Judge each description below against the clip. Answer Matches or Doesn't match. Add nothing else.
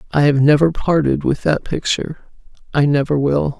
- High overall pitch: Doesn't match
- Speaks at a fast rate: Doesn't match